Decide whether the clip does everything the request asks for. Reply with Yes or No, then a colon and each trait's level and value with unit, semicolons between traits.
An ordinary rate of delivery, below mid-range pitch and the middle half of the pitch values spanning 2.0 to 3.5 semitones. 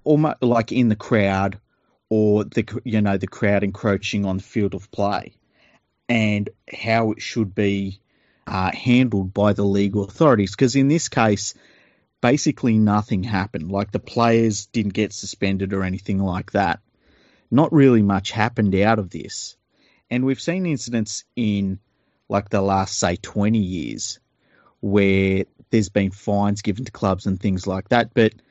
Yes: average, 160 wpm; low, 105 Hz; average, 2.7 semitones